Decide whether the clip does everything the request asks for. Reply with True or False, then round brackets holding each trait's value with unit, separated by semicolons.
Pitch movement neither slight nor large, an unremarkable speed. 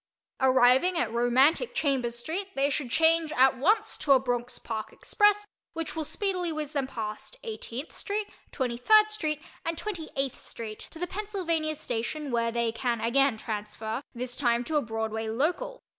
False (5.8 semitones; 160 wpm)